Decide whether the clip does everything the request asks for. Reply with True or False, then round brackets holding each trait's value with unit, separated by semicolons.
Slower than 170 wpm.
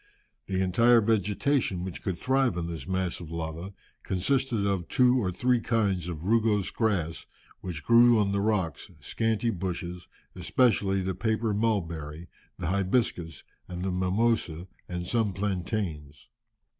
True (140 wpm)